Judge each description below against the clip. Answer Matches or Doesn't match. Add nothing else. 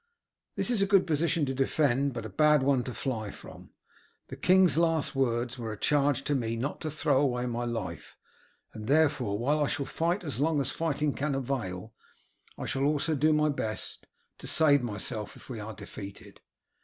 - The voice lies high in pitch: Doesn't match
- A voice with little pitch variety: Doesn't match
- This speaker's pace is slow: Doesn't match